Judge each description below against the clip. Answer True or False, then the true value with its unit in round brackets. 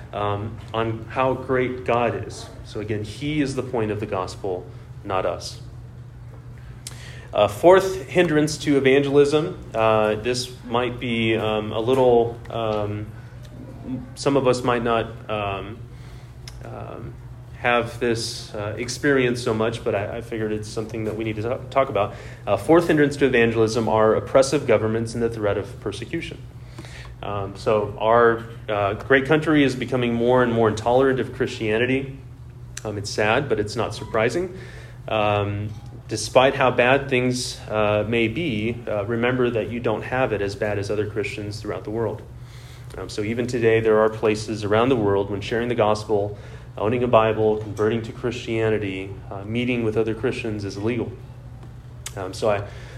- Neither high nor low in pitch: False (115 Hz)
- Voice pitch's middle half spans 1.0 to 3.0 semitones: True (2.5 semitones)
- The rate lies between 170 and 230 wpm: False (160 wpm)